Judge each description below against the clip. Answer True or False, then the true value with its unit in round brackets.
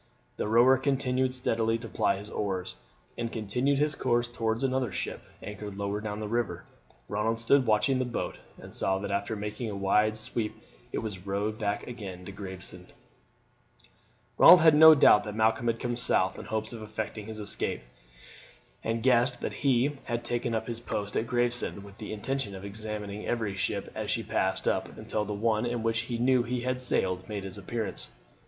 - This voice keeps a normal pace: True (190 wpm)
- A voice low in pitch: True (110 Hz)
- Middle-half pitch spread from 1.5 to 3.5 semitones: True (2.8 semitones)